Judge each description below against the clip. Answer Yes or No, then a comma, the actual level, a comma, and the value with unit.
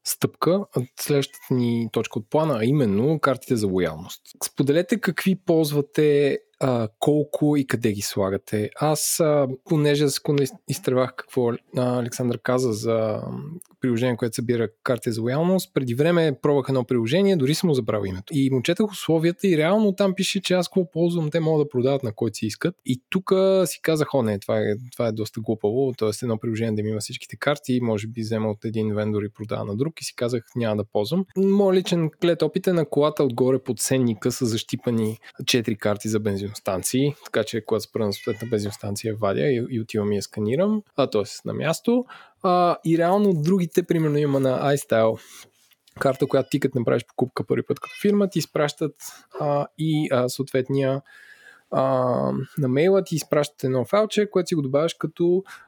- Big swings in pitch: Yes, wide, 6.0 semitones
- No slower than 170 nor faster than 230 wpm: Yes, average, 180 wpm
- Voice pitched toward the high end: No, low, 135 Hz